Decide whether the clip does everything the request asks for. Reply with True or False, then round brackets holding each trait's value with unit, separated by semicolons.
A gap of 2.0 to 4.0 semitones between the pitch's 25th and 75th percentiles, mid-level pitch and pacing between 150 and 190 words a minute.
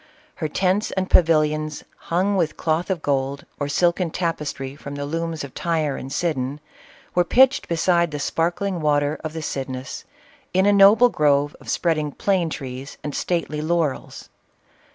True (3.3 semitones; 160 Hz; 155 wpm)